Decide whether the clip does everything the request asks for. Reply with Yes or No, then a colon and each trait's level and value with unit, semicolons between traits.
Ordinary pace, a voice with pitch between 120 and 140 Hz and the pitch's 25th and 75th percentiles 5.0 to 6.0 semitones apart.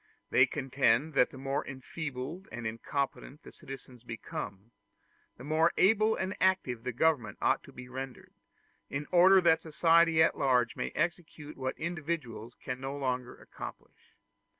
No: average, 150 wpm; low, 135 Hz; average, 4.5 semitones